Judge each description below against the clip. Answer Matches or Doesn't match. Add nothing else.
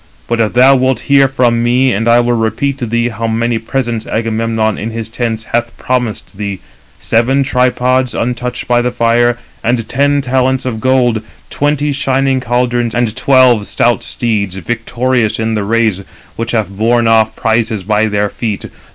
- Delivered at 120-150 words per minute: Doesn't match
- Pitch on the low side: Matches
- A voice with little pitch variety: Matches